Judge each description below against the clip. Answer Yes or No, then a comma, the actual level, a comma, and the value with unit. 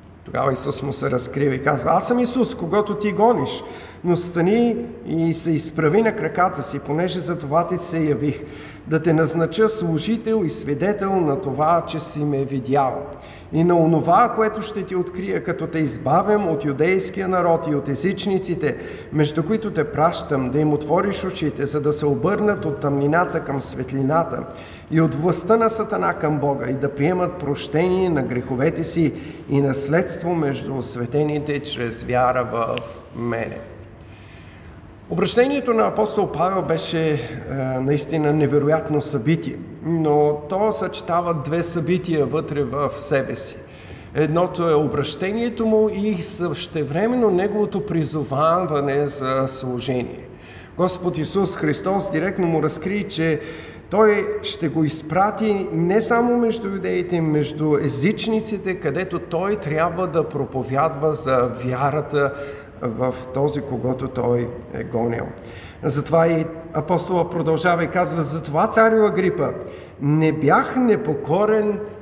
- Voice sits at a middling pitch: Yes, medium, 160 Hz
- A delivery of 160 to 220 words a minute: No, average, 135 wpm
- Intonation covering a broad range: No, average, 4.6 semitones